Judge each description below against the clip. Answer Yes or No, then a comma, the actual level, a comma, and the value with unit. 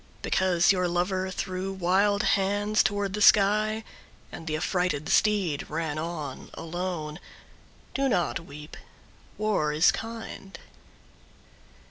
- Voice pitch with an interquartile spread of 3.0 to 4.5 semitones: Yes, average, 3.8 semitones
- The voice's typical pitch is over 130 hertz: Yes, medium, 185 Hz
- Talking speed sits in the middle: No, slow, 110 wpm